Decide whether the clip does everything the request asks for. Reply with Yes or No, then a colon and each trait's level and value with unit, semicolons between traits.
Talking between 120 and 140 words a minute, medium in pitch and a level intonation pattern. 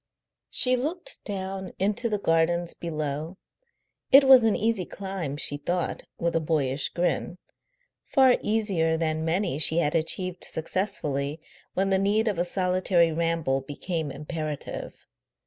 No: slow, 135 wpm; medium, 175 Hz; average, 3.8 semitones